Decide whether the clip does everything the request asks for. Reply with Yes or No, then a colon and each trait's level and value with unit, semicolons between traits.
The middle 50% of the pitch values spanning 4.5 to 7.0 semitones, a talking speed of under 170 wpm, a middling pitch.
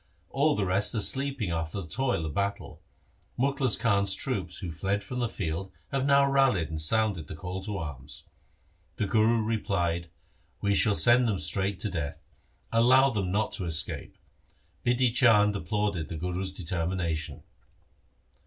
No: average, 5.2 semitones; average, 160 wpm; low, 100 Hz